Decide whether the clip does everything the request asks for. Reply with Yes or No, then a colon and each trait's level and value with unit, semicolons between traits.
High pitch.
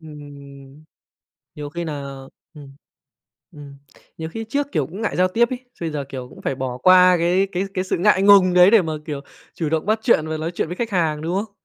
No: medium, 165 Hz